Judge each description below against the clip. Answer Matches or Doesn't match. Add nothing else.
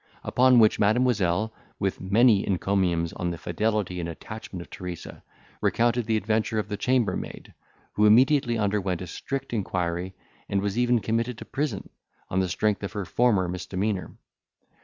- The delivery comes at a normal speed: Matches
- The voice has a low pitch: Matches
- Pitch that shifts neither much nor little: Matches